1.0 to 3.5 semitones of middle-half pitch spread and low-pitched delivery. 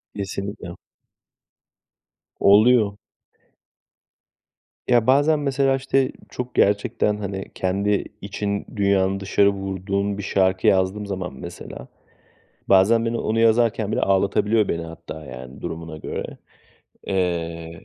Yes: average, 2.8 semitones; low, 100 Hz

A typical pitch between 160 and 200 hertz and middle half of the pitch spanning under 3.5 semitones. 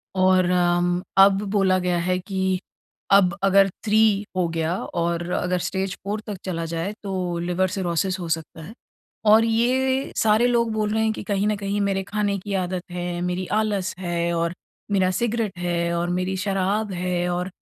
Yes: medium, 185 Hz; narrow, 2.5 semitones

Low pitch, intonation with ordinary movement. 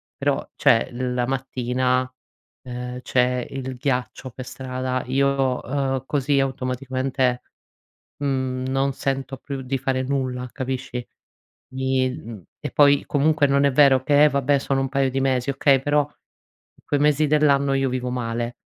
No: low, 130 Hz; narrow, 1.4 semitones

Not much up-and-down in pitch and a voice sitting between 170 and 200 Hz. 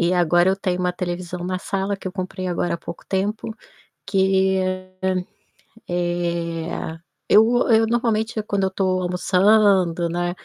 Yes: narrow, 2.1 semitones; medium, 185 Hz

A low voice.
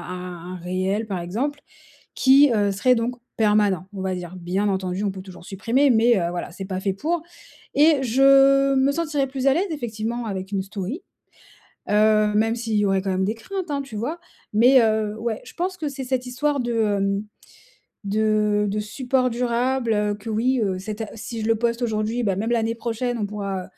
No: high, 220 Hz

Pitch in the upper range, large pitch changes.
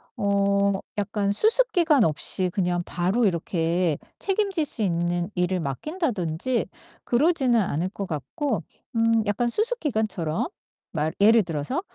Yes: high, 200 Hz; wide, 6.4 semitones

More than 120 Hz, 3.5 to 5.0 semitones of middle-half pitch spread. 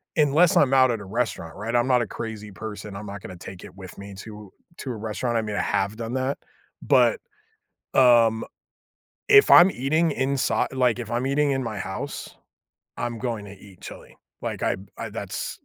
No: low, 115 Hz; average, 4.3 semitones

